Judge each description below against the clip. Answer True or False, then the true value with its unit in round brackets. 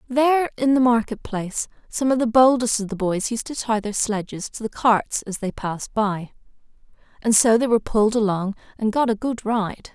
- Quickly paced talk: True (210 wpm)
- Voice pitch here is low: False (225 Hz)